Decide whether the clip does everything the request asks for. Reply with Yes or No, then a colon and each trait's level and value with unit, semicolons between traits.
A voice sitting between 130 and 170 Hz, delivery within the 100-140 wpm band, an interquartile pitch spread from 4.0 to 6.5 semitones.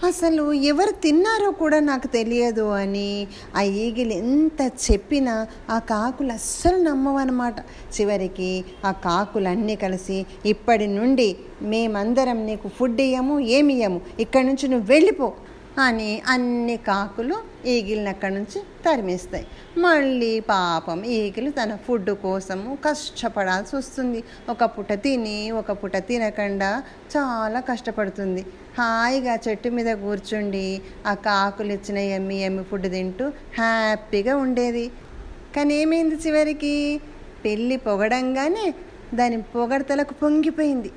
No: high, 230 Hz; average, 105 wpm; average, 5.0 semitones